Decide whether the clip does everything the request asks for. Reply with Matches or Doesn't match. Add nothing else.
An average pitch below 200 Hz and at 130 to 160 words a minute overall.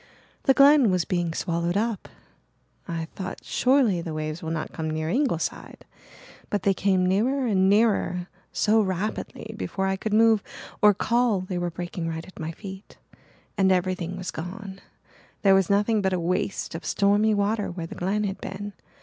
Doesn't match